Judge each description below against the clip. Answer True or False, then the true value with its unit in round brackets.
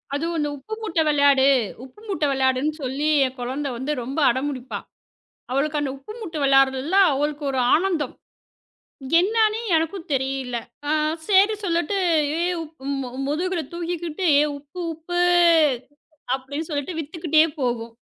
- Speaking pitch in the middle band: False (295 Hz)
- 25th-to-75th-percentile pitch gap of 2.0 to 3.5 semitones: False (4.1 semitones)